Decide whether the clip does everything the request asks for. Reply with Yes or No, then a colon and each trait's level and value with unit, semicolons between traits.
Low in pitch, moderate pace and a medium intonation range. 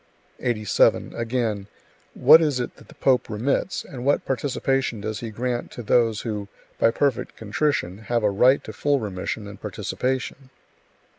Yes: low, 120 Hz; average, 155 wpm; average, 3.7 semitones